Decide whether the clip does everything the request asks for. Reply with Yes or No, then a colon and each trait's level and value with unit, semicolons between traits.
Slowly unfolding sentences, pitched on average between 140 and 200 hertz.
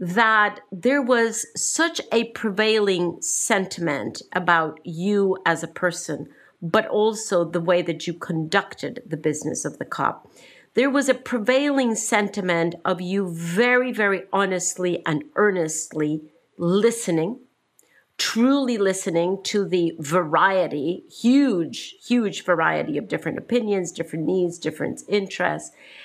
Yes: slow, 120 wpm; high, 190 Hz